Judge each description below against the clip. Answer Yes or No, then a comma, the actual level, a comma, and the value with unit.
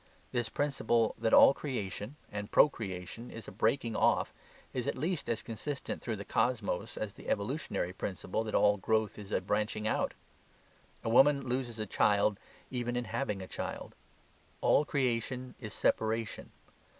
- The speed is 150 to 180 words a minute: Yes, average, 155 wpm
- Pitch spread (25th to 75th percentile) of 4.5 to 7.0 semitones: No, average, 3.4 semitones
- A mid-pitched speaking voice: No, low, 115 Hz